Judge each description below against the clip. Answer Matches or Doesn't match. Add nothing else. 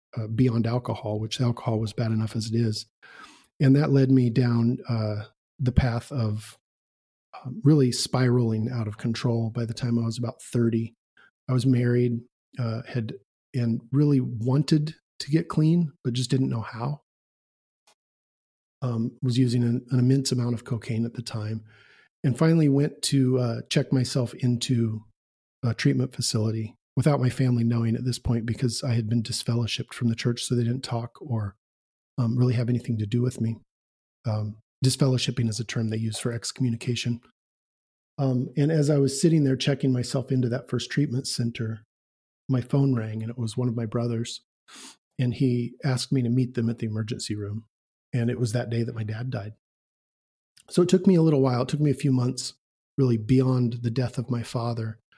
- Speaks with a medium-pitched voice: Doesn't match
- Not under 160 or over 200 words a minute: Matches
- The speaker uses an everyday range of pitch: Doesn't match